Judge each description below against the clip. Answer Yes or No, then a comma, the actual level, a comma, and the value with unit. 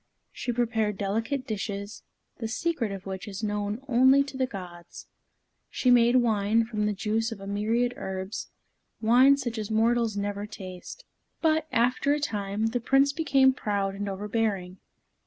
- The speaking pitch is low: No, high, 220 Hz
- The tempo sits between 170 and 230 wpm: No, average, 155 wpm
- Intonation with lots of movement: No, average, 3.5 semitones